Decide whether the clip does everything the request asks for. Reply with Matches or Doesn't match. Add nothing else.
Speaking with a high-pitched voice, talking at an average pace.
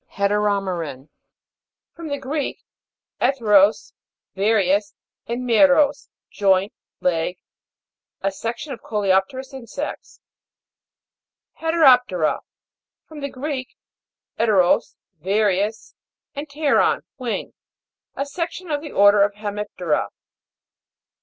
Doesn't match